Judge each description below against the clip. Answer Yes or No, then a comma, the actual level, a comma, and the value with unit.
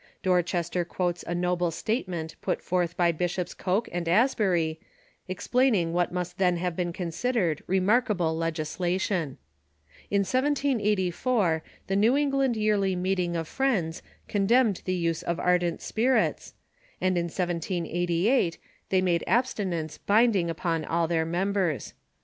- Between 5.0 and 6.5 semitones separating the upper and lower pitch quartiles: No, average, 3.3 semitones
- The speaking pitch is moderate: Yes, medium, 180 Hz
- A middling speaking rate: No, slow, 130 wpm